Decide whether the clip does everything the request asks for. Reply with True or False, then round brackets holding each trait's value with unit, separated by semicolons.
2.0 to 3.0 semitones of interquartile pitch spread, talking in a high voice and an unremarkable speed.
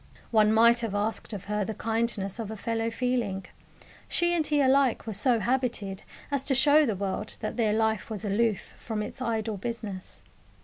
True (2.6 semitones; 225 Hz; 185 wpm)